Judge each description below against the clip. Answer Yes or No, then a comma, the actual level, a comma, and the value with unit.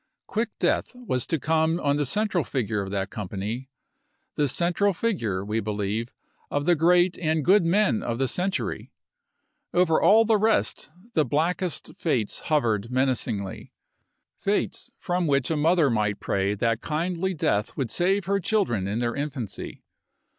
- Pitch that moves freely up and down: Yes, wide, 7.9 semitones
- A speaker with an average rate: Yes, average, 160 wpm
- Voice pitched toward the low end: No, medium, 145 Hz